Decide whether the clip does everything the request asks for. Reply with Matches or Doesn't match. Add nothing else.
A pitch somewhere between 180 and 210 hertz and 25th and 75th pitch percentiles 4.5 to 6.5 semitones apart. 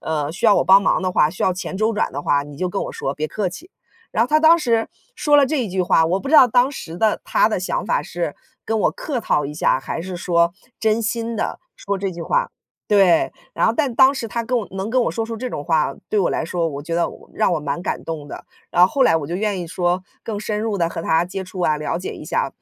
Matches